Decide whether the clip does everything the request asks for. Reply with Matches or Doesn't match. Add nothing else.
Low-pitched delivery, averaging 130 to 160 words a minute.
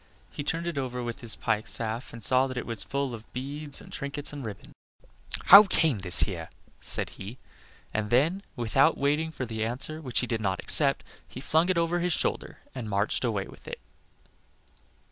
Doesn't match